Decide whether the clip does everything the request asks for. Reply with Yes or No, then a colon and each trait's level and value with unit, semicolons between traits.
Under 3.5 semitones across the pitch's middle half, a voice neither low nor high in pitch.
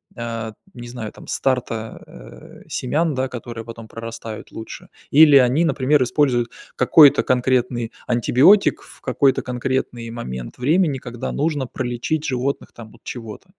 No: average, 2.9 semitones; low, 125 Hz